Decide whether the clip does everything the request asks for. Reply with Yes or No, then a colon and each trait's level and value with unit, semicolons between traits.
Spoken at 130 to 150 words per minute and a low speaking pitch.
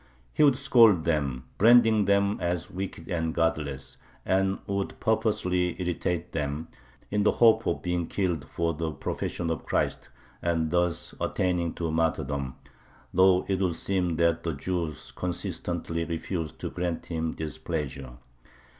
Yes: average, 145 wpm; very low, 85 Hz